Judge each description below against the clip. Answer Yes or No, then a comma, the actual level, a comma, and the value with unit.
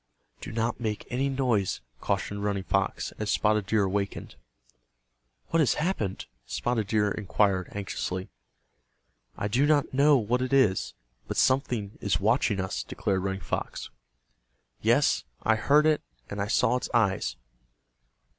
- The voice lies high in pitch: No, low, 110 Hz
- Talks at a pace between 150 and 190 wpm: No, average, 140 wpm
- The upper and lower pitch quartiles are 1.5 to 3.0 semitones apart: No, average, 4.2 semitones